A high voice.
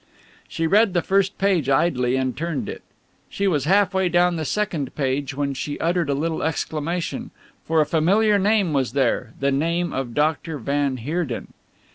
No: medium, 160 Hz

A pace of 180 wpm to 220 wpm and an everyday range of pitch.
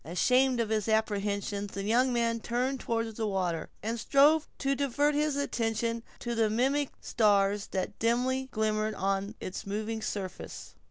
No: average, 155 wpm; average, 3.6 semitones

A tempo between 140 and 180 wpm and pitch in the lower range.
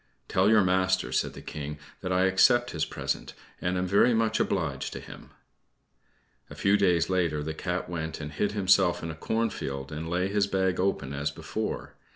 No: average, 190 wpm; very low, 90 Hz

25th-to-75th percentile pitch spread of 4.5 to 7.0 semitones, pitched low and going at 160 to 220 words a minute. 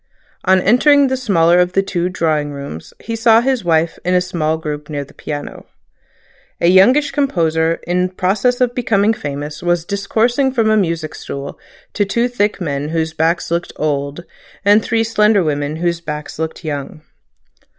No: wide, 5.6 semitones; medium, 175 Hz; average, 170 wpm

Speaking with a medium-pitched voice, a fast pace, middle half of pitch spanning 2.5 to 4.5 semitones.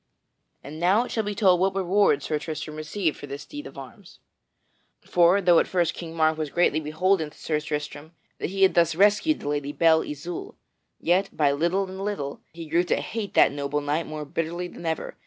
Yes: medium, 165 Hz; fast, 210 wpm; average, 3.7 semitones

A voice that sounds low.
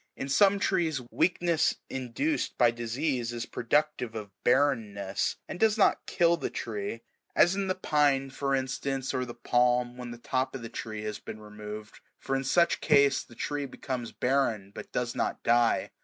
Yes: low, 130 Hz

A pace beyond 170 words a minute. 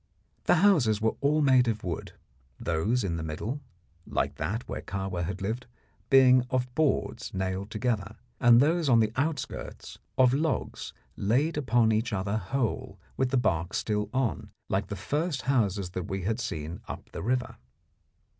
No: average, 165 wpm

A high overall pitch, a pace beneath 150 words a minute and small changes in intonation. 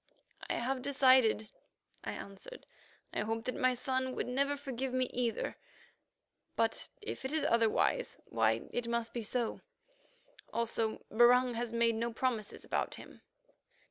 Yes: high, 245 Hz; average, 140 wpm; narrow, 2.2 semitones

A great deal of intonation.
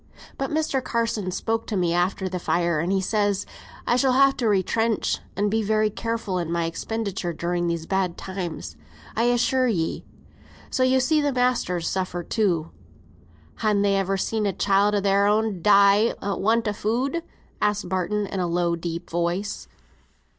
No: average, 4.0 semitones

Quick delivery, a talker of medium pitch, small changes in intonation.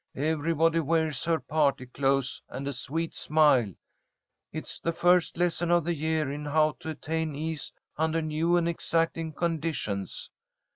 No: average, 145 wpm; medium, 160 Hz; narrow, 2.2 semitones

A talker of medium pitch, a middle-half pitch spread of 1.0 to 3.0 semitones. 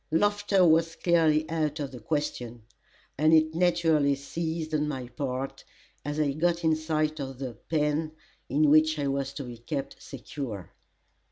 Yes: medium, 155 Hz; average, 2.7 semitones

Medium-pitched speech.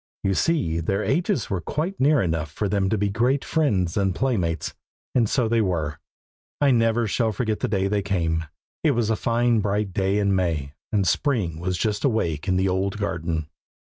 No: low, 100 Hz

